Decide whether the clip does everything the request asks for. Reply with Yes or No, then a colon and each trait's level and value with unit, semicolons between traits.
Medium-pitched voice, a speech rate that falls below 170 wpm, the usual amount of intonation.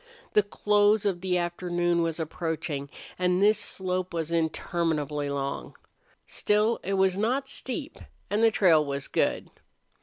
Yes: medium, 180 Hz; average, 140 wpm; average, 4.1 semitones